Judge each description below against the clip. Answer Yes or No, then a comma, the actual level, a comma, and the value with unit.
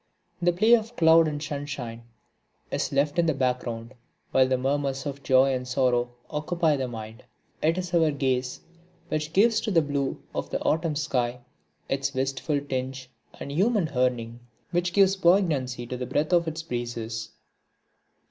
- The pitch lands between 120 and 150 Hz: Yes, medium, 140 Hz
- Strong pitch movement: No, average, 4.4 semitones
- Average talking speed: Yes, average, 160 wpm